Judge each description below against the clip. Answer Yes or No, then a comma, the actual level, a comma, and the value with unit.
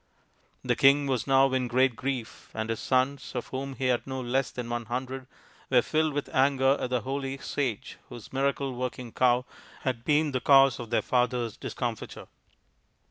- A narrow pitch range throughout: Yes, narrow, 1.9 semitones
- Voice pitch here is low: Yes, low, 130 Hz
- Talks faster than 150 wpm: Yes, average, 180 wpm